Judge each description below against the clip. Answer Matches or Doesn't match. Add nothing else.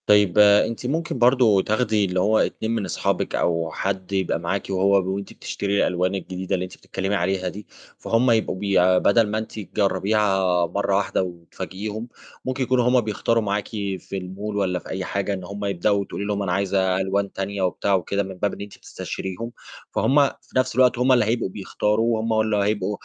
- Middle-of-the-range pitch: Doesn't match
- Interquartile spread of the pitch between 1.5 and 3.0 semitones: Matches